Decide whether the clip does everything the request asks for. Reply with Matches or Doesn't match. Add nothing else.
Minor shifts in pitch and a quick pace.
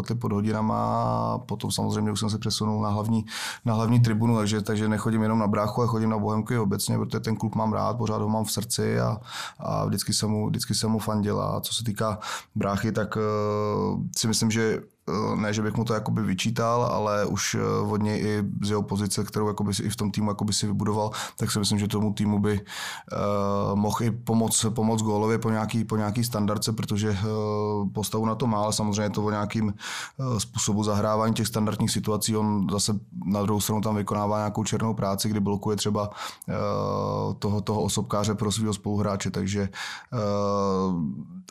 Matches